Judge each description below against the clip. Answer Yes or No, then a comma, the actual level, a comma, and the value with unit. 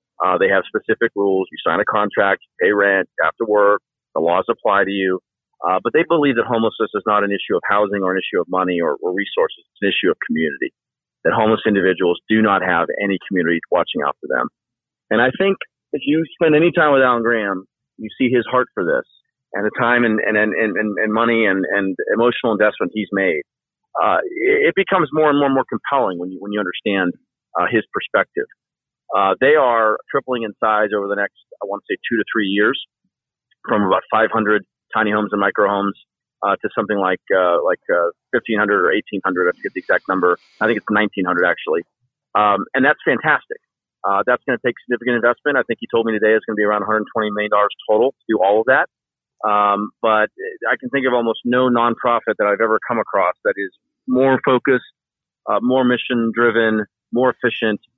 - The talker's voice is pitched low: Yes, low, 110 Hz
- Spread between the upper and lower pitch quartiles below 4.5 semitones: Yes, average, 3.8 semitones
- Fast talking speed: Yes, fast, 210 wpm